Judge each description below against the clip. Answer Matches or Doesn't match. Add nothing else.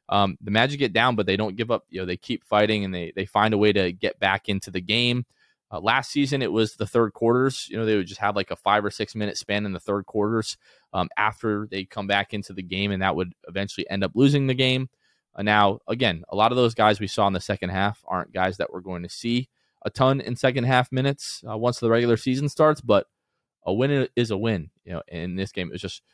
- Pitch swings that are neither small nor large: Matches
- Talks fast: Matches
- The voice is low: Matches